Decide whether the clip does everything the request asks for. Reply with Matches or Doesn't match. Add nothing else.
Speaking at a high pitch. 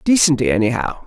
Doesn't match